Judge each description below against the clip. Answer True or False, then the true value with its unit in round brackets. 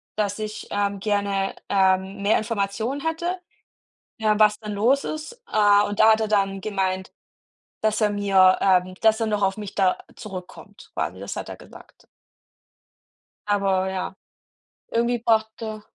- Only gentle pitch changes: True (2.0 semitones)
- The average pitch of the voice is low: False (205 Hz)